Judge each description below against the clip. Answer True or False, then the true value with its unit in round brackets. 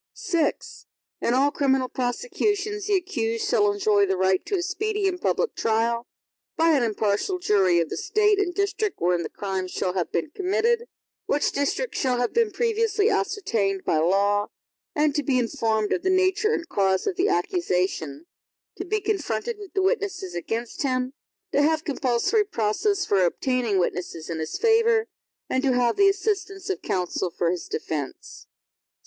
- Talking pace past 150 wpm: True (170 wpm)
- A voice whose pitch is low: False (280 Hz)